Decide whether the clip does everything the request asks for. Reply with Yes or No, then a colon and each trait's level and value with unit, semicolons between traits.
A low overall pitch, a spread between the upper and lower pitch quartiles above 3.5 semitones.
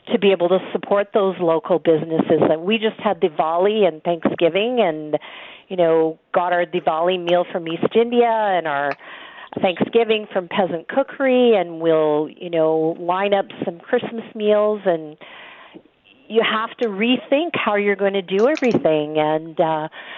No: high, 190 Hz; average, 5.1 semitones